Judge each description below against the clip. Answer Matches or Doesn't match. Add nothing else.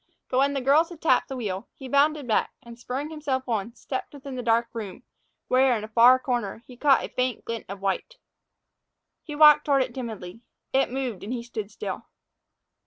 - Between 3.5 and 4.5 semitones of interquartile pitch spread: Doesn't match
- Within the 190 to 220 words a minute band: Matches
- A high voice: Matches